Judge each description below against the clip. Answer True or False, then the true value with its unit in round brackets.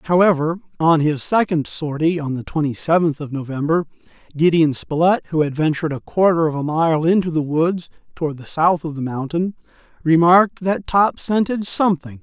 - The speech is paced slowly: False (170 wpm)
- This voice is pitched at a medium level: True (160 Hz)